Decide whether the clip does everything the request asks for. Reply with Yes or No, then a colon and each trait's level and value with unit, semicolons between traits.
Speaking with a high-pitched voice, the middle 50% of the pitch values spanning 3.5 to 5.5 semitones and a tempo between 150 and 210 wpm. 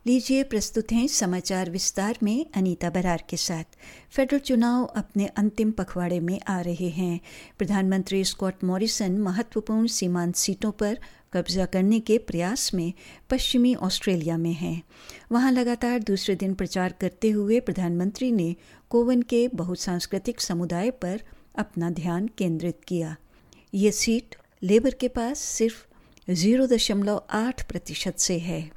No: high, 195 Hz; average, 4.2 semitones; slow, 135 wpm